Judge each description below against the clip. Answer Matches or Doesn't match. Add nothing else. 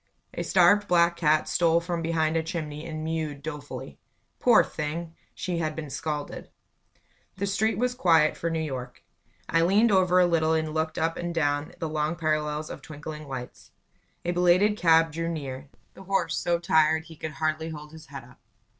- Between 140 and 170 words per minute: Doesn't match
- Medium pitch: Matches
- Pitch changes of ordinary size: Doesn't match